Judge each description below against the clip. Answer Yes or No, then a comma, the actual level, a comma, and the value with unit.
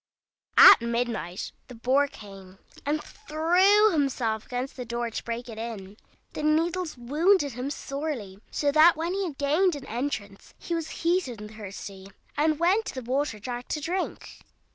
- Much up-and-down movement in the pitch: Yes, wide, 5.7 semitones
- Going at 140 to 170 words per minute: Yes, average, 165 wpm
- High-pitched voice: Yes, very high, 275 Hz